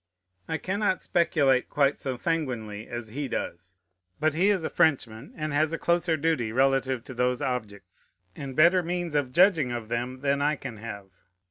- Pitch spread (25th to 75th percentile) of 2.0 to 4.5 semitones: No, average, 5.1 semitones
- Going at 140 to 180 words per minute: Yes, average, 175 wpm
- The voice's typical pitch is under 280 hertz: Yes, low, 135 Hz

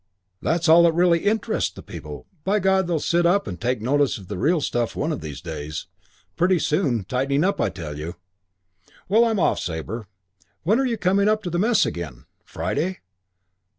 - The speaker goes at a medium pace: Yes, average, 190 wpm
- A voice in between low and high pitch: Yes, medium, 160 Hz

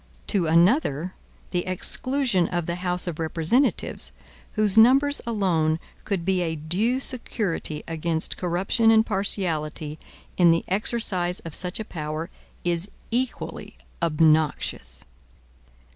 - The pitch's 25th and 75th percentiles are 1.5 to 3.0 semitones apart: No, average, 4.8 semitones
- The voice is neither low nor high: Yes, medium, 180 Hz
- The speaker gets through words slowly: Yes, slow, 115 wpm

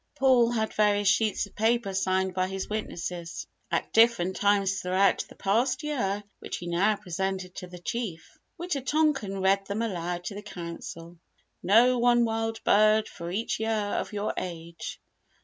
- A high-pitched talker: Yes, high, 200 Hz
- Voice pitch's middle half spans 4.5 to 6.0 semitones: No, average, 3.4 semitones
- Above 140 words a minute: Yes, average, 165 wpm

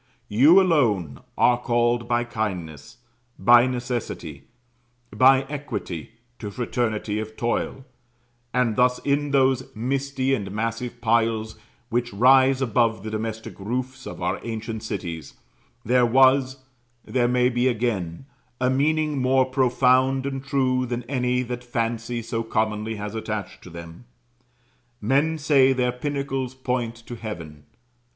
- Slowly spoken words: Yes, slow, 130 wpm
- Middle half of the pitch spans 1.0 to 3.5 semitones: Yes, average, 2.9 semitones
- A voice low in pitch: Yes, low, 120 Hz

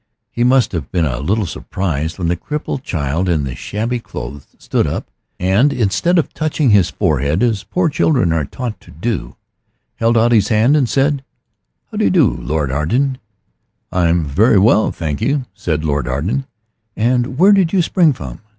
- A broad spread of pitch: Yes, wide, 8.8 semitones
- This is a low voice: Yes, low, 105 Hz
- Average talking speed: Yes, average, 185 wpm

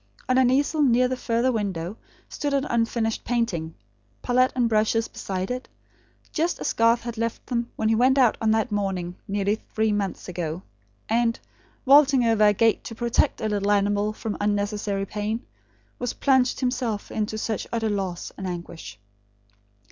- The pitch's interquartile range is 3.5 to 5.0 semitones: No, average, 3.1 semitones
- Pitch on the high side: Yes, high, 220 Hz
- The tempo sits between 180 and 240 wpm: No, average, 165 wpm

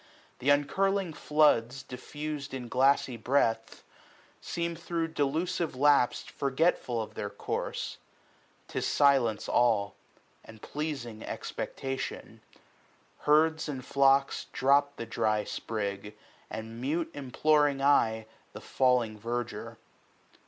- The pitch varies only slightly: No, average, 4.3 semitones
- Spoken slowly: Yes, slow, 105 wpm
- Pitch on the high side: No, low, 135 Hz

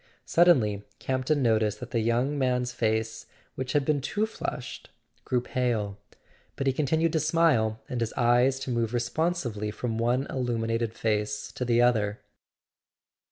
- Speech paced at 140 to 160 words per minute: Yes, average, 150 wpm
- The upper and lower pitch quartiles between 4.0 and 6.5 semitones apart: No, average, 3.3 semitones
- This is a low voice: Yes, low, 120 Hz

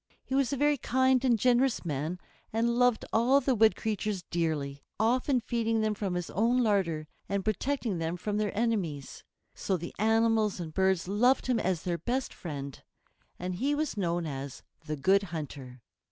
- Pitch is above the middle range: Yes, high, 210 Hz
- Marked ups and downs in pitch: Yes, wide, 5.9 semitones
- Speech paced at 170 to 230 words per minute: Yes, average, 175 wpm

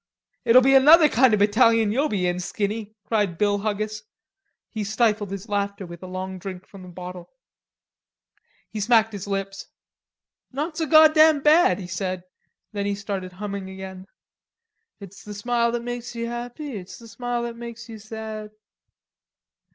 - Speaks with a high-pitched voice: Yes, high, 215 Hz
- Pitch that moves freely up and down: No, average, 3.4 semitones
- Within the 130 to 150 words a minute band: No, average, 165 wpm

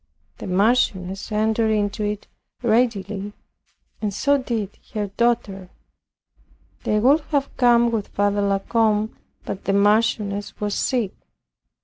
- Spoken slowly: Yes, slow, 120 wpm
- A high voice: Yes, high, 210 Hz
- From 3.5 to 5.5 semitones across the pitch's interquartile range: No, narrow, 2.5 semitones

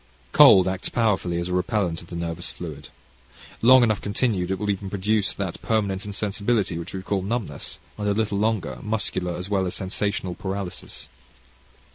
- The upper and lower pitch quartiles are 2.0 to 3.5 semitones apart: Yes, average, 2.7 semitones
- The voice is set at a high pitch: No, very low, 95 Hz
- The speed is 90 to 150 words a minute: No, average, 170 wpm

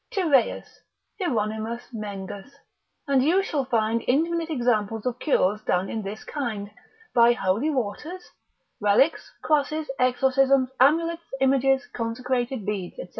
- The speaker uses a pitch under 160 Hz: No, very high, 250 Hz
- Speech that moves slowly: Yes, slow, 125 wpm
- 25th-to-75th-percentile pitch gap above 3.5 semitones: Yes, average, 4.6 semitones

